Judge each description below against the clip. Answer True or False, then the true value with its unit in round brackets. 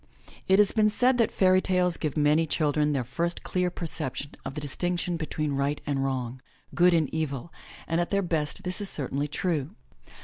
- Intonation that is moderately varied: True (3.8 semitones)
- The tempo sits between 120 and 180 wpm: False (190 wpm)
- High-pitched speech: False (160 Hz)